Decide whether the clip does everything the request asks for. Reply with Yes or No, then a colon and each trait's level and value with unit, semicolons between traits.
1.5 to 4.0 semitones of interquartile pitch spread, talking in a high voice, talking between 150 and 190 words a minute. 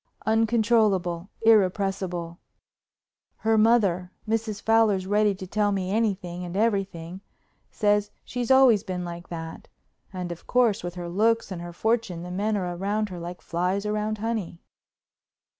No: average, 3.5 semitones; high, 200 Hz; slow, 135 wpm